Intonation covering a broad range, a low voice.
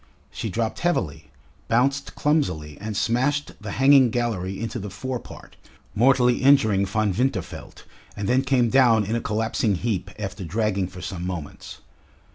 No: average, 4.7 semitones; low, 110 Hz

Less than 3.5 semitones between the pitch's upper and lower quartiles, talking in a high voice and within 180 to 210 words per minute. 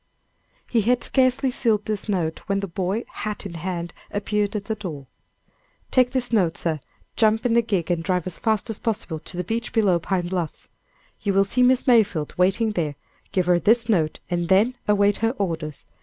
No: average, 4.3 semitones; high, 200 Hz; average, 195 wpm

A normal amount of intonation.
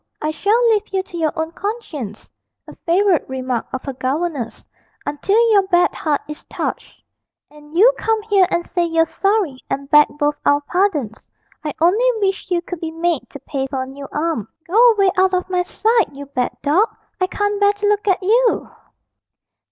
No: wide, 5.7 semitones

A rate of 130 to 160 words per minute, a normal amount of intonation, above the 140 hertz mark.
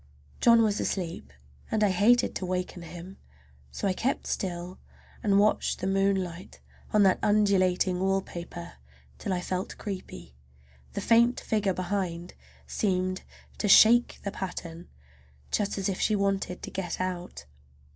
No: average, 140 wpm; narrow, 2.1 semitones; high, 190 Hz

